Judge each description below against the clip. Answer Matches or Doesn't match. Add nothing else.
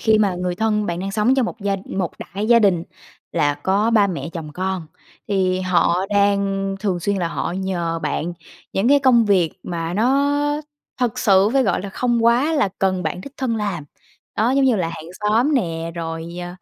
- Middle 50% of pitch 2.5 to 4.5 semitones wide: Matches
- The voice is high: Matches